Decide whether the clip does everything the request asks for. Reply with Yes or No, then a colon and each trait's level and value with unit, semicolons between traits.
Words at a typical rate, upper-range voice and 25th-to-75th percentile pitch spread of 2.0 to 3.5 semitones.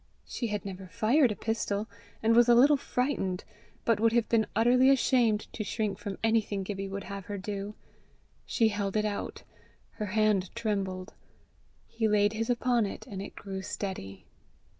Yes: average, 170 wpm; high, 210 Hz; narrow, 2.6 semitones